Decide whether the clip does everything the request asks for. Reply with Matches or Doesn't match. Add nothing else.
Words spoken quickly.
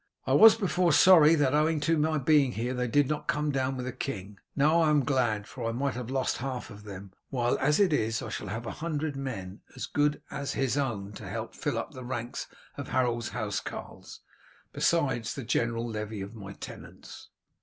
Matches